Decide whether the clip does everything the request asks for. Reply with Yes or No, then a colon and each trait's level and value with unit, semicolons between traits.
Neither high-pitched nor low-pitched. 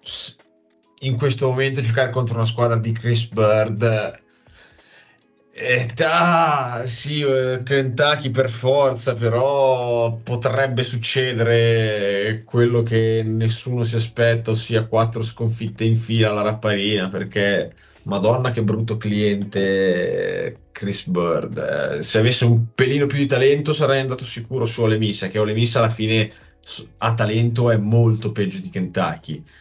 No: low, 115 Hz